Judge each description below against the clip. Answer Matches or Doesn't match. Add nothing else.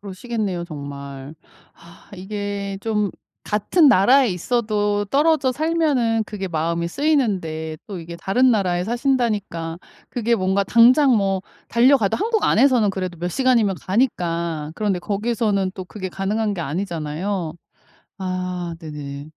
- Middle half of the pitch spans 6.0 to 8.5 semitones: Doesn't match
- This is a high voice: Matches